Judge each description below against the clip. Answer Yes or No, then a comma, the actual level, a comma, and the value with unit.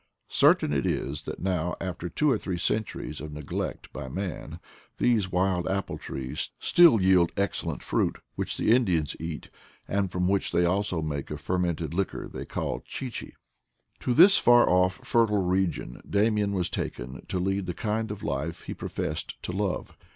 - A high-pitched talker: No, very low, 95 Hz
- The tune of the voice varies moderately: Yes, average, 3.4 semitones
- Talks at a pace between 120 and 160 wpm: No, average, 170 wpm